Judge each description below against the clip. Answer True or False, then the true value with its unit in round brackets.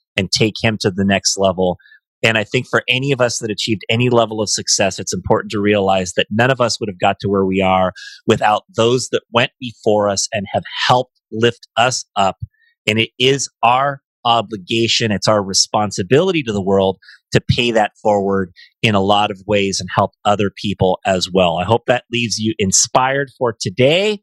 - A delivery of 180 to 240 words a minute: True (200 wpm)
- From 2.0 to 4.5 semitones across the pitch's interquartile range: True (3.3 semitones)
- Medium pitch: False (110 Hz)